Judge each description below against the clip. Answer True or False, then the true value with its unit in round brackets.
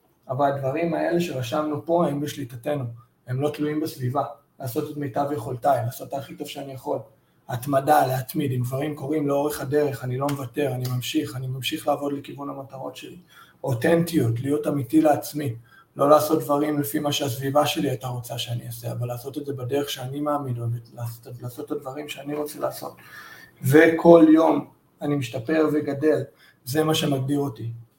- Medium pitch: True (145 Hz)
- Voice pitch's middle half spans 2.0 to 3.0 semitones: True (2.4 semitones)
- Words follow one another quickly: True (165 wpm)